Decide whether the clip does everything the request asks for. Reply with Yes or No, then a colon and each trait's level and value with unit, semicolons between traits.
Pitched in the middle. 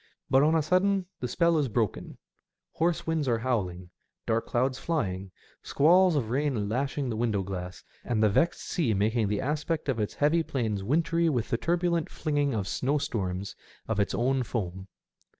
No: low, 130 Hz